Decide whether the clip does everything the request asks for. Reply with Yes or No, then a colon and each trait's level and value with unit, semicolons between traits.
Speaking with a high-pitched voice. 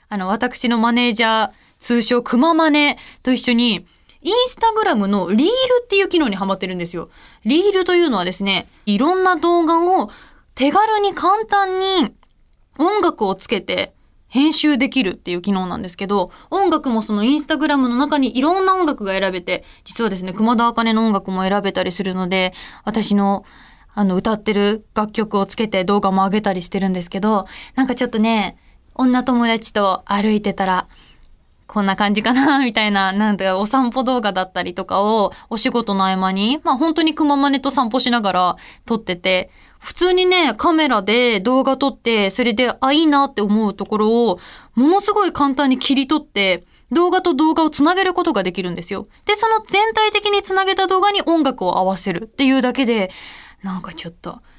Yes: high, 235 Hz